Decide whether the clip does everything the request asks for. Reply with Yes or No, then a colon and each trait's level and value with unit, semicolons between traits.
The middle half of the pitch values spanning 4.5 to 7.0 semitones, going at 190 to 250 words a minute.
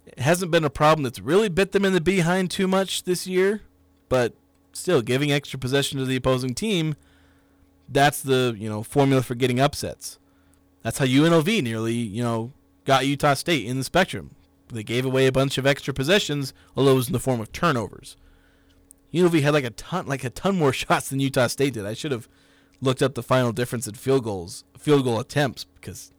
Yes: average, 4.9 semitones; fast, 205 wpm